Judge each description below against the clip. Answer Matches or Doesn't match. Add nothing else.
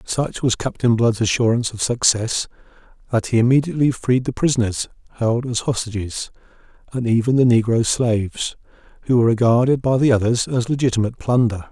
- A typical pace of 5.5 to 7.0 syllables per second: Matches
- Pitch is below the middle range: Matches